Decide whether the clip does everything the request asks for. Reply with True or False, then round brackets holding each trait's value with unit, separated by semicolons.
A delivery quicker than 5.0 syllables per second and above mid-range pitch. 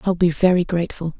False (6.5 syllables/s; 175 Hz)